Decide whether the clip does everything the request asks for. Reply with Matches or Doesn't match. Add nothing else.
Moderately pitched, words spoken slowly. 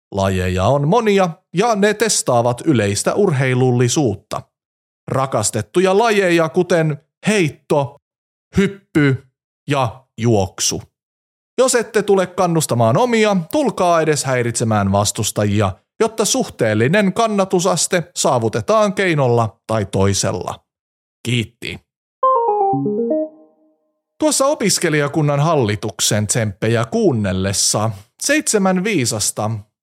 Matches